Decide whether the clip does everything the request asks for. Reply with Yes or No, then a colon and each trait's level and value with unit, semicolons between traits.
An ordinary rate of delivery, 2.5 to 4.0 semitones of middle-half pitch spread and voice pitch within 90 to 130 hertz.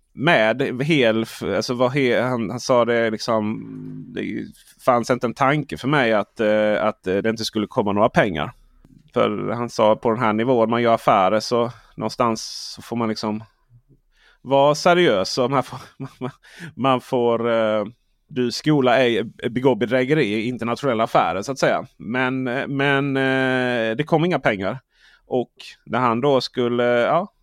Yes: average, 155 wpm; average, 2.8 semitones; low, 120 Hz